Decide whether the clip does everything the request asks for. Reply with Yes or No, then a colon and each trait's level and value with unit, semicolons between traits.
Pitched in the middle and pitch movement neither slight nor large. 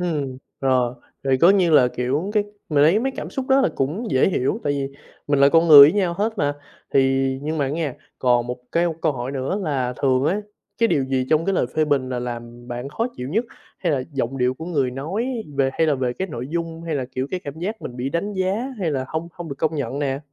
Yes: medium, 145 Hz; average, 4.7 semitones